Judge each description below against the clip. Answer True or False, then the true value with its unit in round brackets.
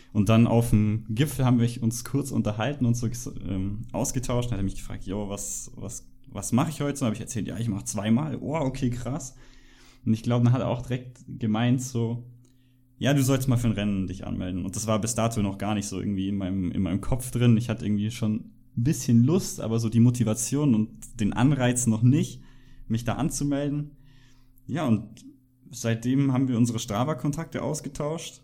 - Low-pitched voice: True (120 Hz)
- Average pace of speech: False (205 wpm)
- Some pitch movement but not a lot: True (3.2 semitones)